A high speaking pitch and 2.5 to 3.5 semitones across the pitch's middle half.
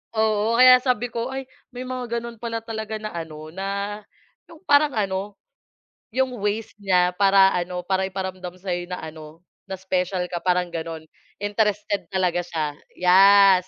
No: high, 195 Hz; average, 3.9 semitones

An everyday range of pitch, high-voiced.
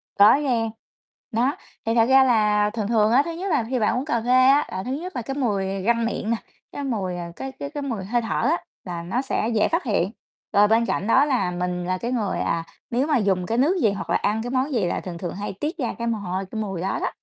Yes: average, 4.9 semitones; high, 225 Hz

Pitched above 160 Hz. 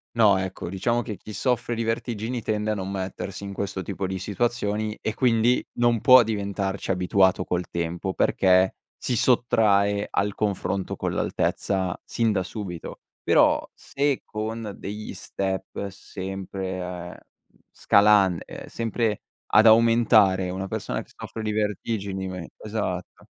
No: low, 100 Hz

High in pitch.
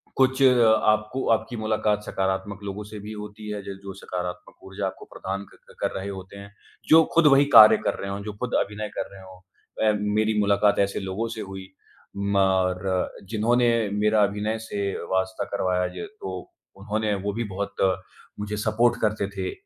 No: low, 105 Hz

